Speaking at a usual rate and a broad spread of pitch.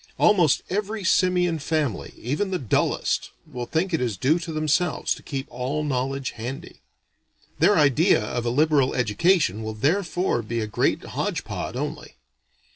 Yes: average, 155 wpm; wide, 6.1 semitones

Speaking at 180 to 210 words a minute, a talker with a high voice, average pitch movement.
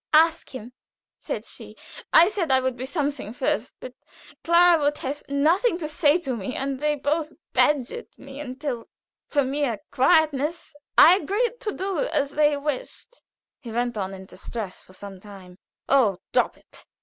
No: average, 165 wpm; very high, 285 Hz; average, 4.3 semitones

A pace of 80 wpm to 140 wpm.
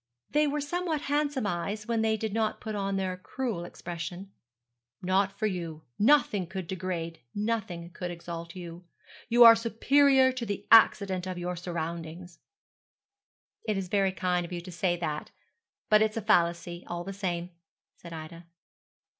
No: average, 155 wpm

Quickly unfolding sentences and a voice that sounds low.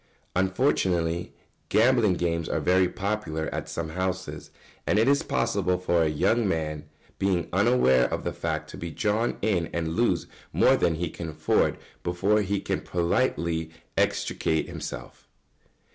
No: average, 150 wpm; very low, 90 Hz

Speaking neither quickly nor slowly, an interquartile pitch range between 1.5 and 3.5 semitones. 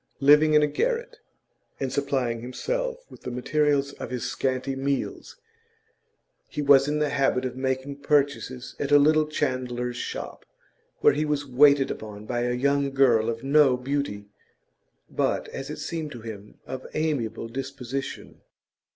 Yes: average, 150 wpm; average, 2.7 semitones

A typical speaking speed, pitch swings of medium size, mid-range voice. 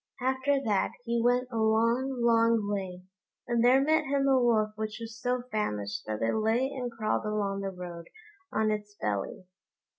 No: average, 175 wpm; average, 3.3 semitones; high, 225 Hz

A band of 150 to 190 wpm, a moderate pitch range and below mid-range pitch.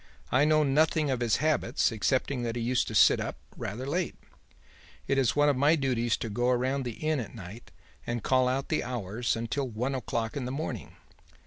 No: fast, 205 wpm; average, 3.1 semitones; low, 130 Hz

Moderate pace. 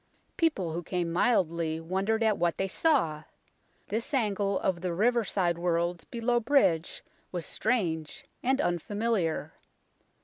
No: slow, 125 wpm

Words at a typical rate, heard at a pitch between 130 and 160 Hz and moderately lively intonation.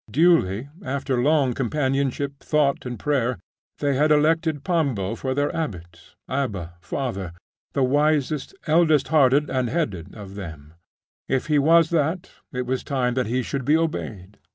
Yes: average, 150 wpm; low, 135 Hz; average, 4.2 semitones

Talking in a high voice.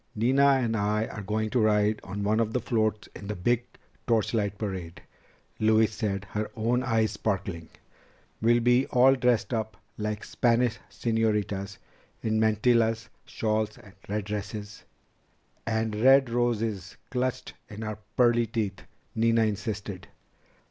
No: low, 110 Hz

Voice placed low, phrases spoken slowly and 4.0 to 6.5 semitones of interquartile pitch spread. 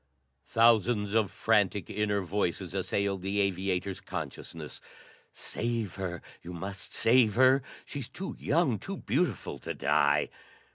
No: low, 105 Hz; slow, 125 wpm; average, 3.4 semitones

